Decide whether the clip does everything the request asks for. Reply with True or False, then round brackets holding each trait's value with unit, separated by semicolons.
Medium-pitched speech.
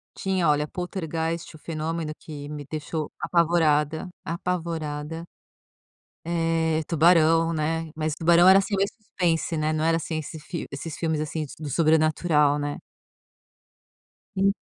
True (160 Hz)